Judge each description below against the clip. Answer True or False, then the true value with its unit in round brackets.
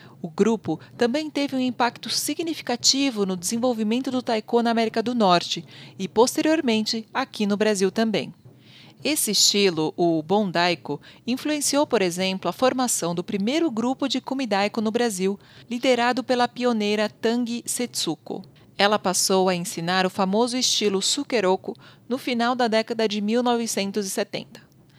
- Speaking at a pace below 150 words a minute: True (135 wpm)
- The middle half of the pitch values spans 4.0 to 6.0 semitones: True (4.5 semitones)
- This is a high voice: True (225 Hz)